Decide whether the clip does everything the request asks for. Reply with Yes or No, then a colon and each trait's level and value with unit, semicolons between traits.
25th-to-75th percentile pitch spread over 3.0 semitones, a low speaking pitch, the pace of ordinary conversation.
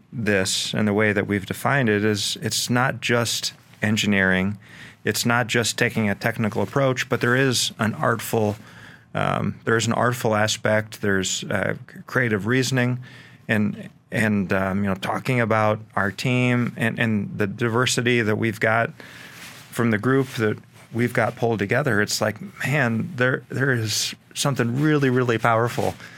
No: average, 2.7 semitones; low, 115 Hz; average, 155 wpm